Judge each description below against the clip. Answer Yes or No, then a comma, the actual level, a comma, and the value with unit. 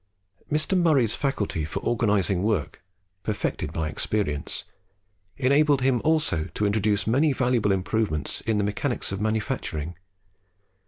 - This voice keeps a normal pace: No, slow, 120 wpm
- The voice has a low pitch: Yes, low, 110 Hz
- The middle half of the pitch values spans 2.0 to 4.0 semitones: No, wide, 5.4 semitones